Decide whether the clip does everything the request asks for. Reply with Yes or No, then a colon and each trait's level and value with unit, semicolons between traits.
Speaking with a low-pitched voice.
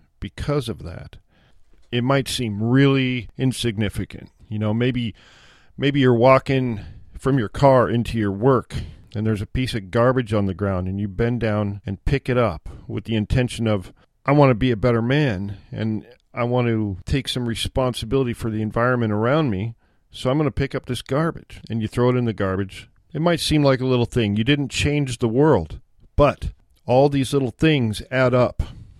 Yes: low, 120 Hz